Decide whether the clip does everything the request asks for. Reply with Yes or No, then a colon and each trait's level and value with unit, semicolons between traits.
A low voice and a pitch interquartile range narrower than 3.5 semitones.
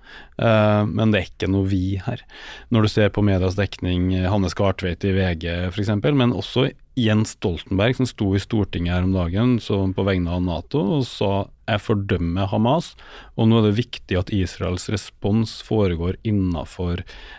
Yes: low, 100 Hz; average, 2.9 semitones